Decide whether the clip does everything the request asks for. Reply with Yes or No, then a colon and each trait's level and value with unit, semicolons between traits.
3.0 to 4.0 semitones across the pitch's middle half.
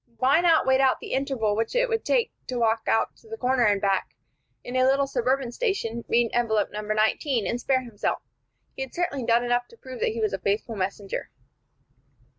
Yes: average, 3.5 semitones